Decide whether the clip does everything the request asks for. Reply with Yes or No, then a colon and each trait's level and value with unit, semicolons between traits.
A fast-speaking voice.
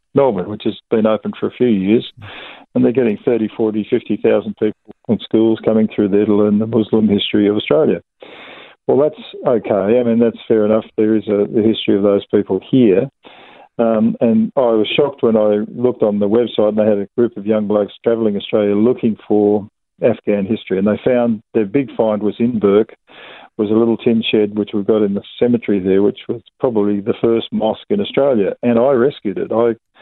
Yes: fast, 210 wpm